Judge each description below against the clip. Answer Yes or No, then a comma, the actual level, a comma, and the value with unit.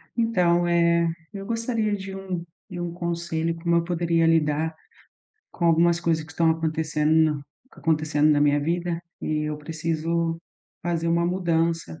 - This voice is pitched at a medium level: Yes, medium, 170 Hz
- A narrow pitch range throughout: Yes, narrow, 1.4 semitones